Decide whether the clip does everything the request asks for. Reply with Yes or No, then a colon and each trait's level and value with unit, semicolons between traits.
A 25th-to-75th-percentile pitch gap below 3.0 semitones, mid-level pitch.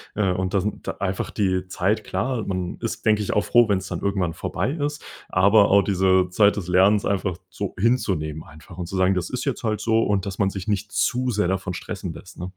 No: narrow, 2.5 semitones; low, 100 Hz